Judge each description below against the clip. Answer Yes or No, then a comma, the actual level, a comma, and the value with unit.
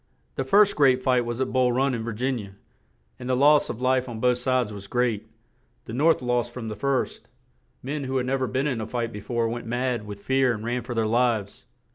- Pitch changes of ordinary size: No, narrow, 2.2 semitones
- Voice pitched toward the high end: No, low, 125 Hz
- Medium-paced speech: No, fast, 245 wpm